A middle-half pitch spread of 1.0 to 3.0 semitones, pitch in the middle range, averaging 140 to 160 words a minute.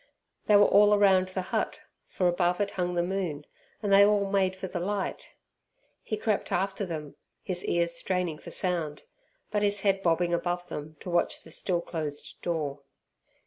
No: narrow, 2.4 semitones; medium, 180 Hz; average, 180 wpm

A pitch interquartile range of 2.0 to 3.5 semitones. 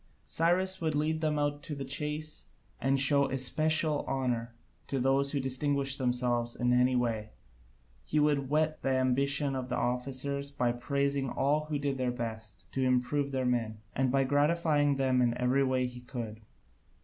Yes: average, 2.7 semitones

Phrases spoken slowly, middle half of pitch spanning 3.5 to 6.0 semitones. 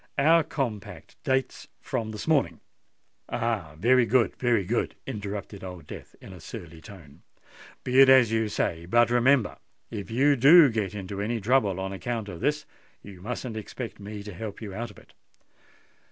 No: average, 165 wpm; average, 4.3 semitones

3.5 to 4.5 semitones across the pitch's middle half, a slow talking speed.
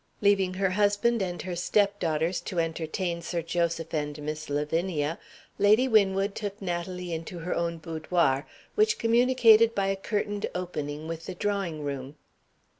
No: average, 3.8 semitones; average, 145 wpm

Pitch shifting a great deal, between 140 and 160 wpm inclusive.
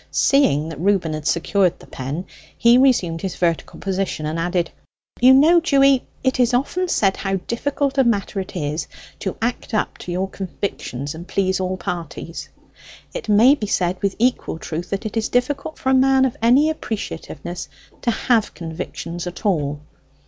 No: wide, 6.5 semitones; average, 175 wpm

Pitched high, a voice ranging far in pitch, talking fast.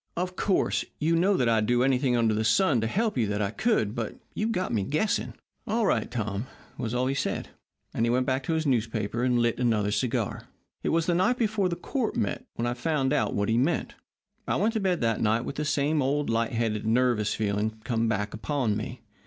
No: low, 125 Hz; wide, 6.2 semitones; fast, 225 wpm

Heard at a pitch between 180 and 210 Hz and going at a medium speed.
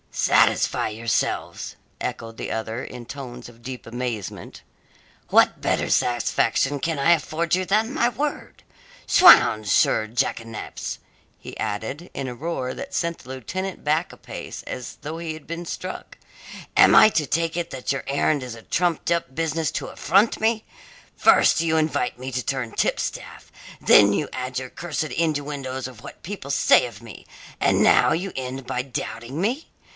No: medium, 140 Hz; average, 165 wpm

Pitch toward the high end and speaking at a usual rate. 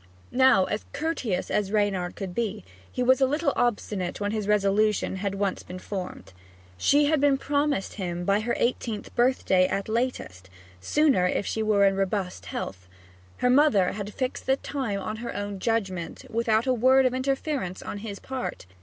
Yes: high, 215 Hz; average, 170 wpm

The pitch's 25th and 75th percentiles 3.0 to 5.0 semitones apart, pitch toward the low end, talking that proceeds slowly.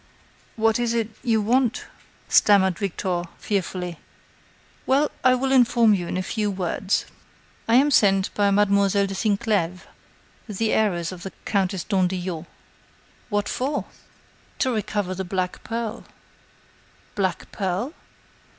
No: average, 3.4 semitones; high, 200 Hz; slow, 125 wpm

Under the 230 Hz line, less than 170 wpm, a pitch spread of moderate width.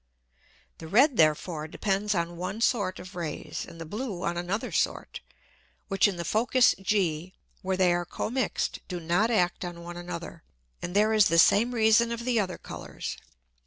No: medium, 185 Hz; average, 175 wpm; average, 3.9 semitones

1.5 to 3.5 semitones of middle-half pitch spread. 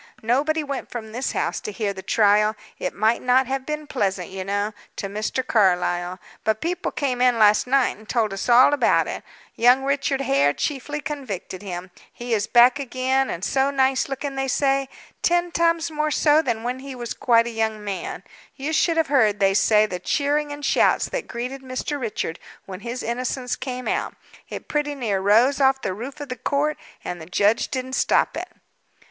No: average, 4.7 semitones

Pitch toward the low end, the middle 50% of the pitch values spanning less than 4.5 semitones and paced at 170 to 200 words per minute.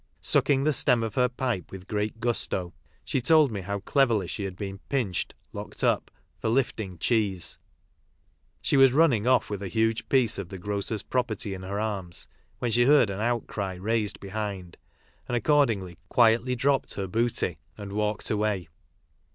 Yes: low, 110 Hz; average, 3.8 semitones; average, 175 wpm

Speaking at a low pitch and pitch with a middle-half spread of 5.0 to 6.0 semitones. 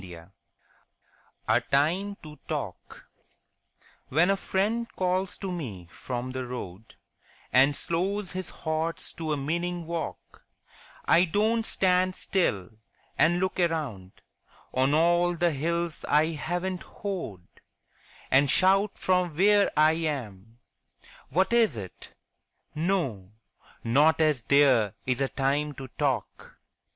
No: medium, 160 Hz; wide, 5.6 semitones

